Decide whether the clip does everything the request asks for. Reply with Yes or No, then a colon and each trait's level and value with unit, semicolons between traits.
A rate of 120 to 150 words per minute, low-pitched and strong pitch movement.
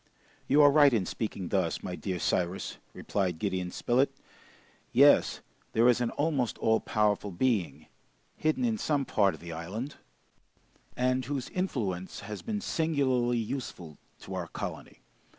Yes: average, 145 wpm; low, 115 Hz; wide, 6.8 semitones